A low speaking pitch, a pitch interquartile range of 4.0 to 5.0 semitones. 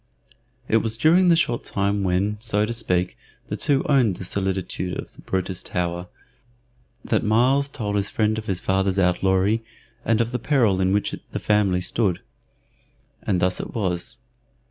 No: low, 100 Hz; average, 3.6 semitones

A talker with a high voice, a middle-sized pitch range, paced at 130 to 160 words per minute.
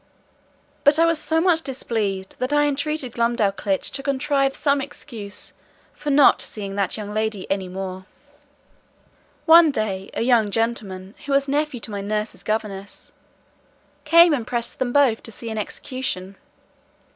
No: high, 235 Hz; wide, 5.9 semitones; average, 150 wpm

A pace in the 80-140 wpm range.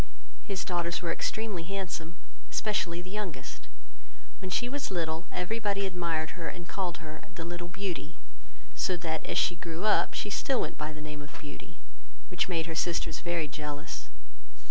No: average, 170 wpm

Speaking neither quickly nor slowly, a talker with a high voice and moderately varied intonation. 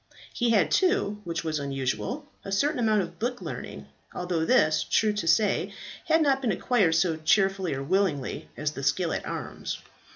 No: average, 175 wpm; high, 195 Hz; wide, 6.8 semitones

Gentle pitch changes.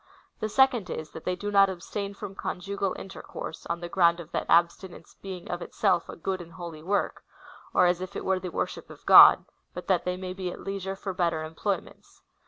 Yes: narrow, 2.2 semitones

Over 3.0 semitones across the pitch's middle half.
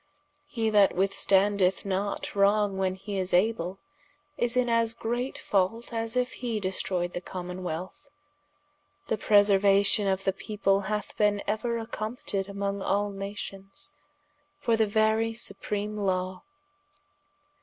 No: narrow, 2.5 semitones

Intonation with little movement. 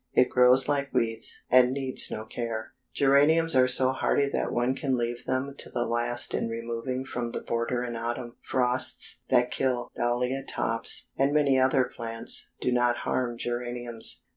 Yes: narrow, 1.8 semitones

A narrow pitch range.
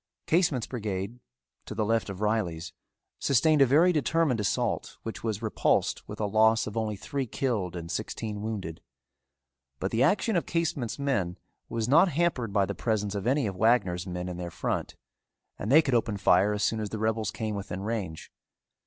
No: average, 4.4 semitones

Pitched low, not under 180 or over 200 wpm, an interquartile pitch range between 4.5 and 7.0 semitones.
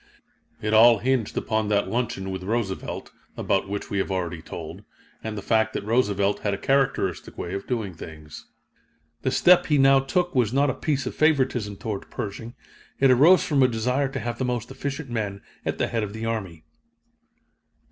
Yes: low, 115 Hz; average, 190 wpm; average, 4.8 semitones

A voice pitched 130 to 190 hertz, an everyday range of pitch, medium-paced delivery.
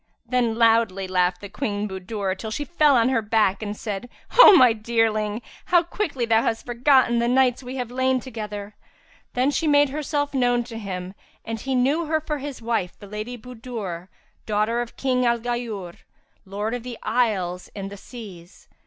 No: high, 230 Hz; average, 3.5 semitones; average, 180 wpm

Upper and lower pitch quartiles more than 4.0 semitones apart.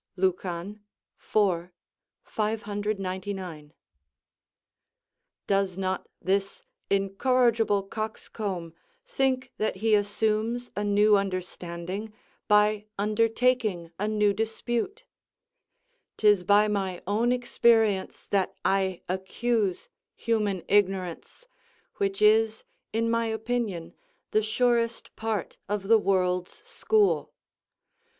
No: average, 2.7 semitones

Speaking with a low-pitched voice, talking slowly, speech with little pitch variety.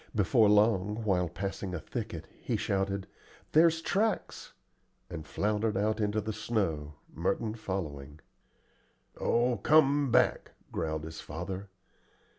No: low, 100 Hz; slow, 115 wpm; average, 4.1 semitones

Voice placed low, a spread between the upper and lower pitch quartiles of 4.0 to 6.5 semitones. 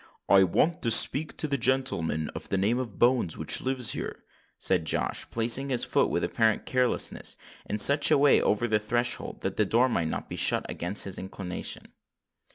Yes: low, 115 Hz; average, 5.0 semitones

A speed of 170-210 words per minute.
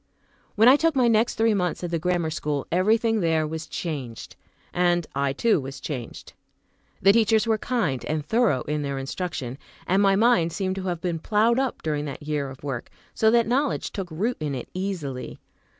Yes: average, 195 wpm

